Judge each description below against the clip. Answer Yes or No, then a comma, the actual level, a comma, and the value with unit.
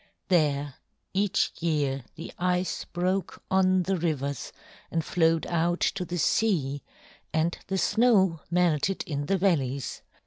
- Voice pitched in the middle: Yes, medium, 170 Hz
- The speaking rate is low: Yes, slow, 130 wpm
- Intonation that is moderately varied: Yes, average, 3.9 semitones